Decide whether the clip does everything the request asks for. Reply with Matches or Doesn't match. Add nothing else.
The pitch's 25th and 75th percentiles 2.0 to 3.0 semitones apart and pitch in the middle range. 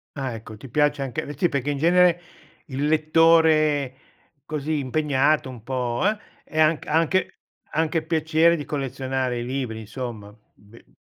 Doesn't match